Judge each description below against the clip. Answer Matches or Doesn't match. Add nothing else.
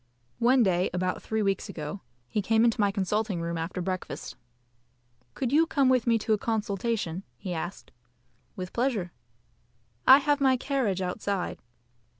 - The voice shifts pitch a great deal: Doesn't match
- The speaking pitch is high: Matches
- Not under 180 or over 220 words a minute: Doesn't match